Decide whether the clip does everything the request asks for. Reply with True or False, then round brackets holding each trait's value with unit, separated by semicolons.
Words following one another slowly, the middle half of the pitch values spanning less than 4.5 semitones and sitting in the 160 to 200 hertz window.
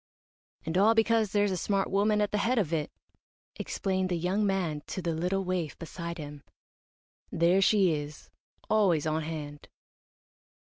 False (160 wpm; 3.9 semitones; 185 Hz)